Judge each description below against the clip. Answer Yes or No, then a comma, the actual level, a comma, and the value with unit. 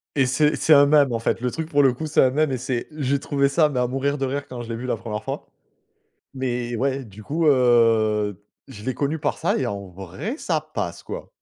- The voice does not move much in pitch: No, average, 3.5 semitones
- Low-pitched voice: Yes, low, 130 Hz